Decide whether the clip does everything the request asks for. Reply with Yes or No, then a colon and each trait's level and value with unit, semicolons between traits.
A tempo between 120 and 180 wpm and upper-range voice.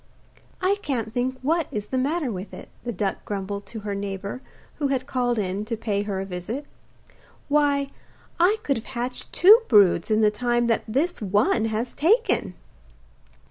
Yes: average, 175 wpm; high, 235 Hz